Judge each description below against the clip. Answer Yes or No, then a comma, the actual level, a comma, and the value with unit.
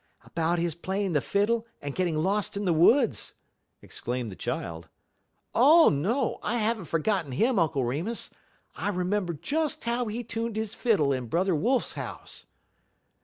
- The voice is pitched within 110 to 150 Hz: No, high, 195 Hz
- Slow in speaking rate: No, average, 160 wpm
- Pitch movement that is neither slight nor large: No, wide, 6.5 semitones